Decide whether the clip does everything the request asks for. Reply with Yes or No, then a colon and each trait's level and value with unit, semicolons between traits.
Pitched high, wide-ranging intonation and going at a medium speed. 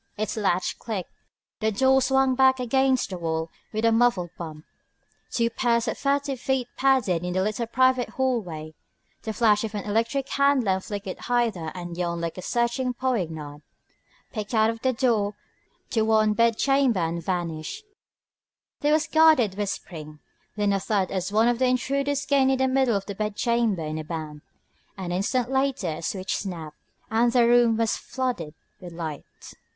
Yes: high, 220 Hz; wide, 6.0 semitones; average, 170 wpm